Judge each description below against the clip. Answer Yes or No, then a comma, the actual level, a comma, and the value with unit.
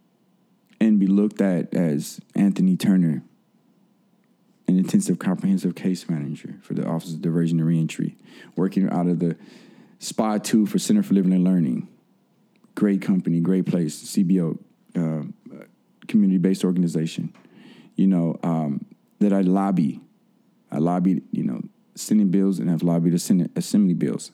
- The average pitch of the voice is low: Yes, low, 100 Hz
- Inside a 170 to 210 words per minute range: No, average, 140 wpm